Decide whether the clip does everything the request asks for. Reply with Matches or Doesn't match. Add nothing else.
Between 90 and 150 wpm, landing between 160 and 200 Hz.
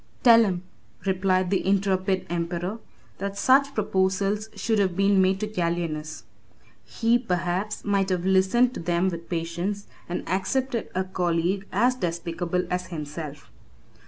Matches